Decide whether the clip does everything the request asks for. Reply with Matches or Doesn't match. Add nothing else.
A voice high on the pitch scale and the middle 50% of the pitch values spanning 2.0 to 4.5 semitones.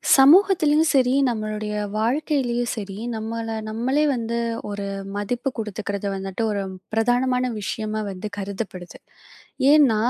Matches